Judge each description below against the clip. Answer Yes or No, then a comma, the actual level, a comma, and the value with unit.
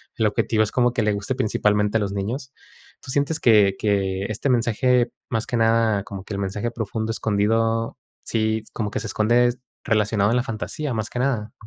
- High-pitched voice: No, low, 110 Hz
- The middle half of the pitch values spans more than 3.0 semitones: No, narrow, 2.4 semitones